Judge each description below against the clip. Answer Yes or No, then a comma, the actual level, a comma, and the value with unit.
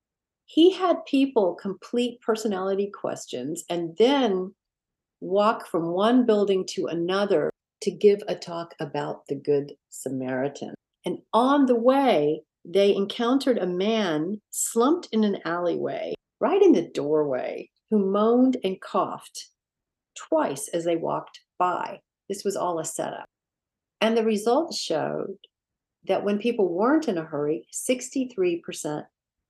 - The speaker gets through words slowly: Yes, slow, 130 wpm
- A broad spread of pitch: Yes, wide, 5.9 semitones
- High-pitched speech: Yes, high, 200 Hz